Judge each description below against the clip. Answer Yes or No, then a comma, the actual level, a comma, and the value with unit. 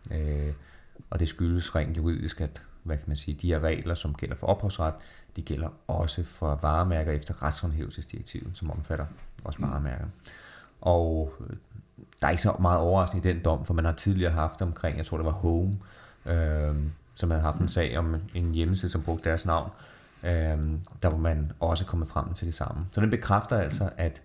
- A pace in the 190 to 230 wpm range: Yes, average, 195 wpm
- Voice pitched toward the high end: No, very low, 85 Hz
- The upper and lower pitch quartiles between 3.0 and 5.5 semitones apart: No, narrow, 2.4 semitones